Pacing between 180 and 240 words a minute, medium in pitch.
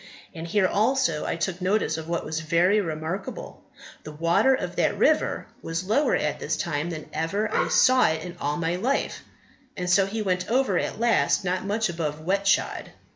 Yes: average, 185 wpm; medium, 180 Hz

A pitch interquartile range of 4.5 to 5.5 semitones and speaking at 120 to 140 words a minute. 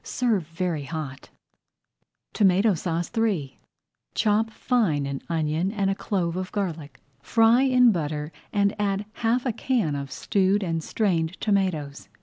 Yes: average, 5.2 semitones; slow, 135 wpm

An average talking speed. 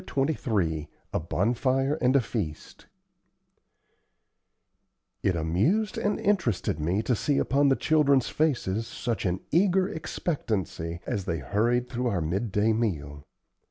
No: slow, 125 wpm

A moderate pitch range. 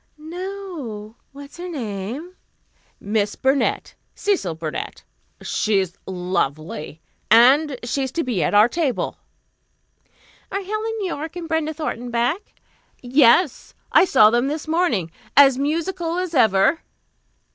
No: wide, 7.7 semitones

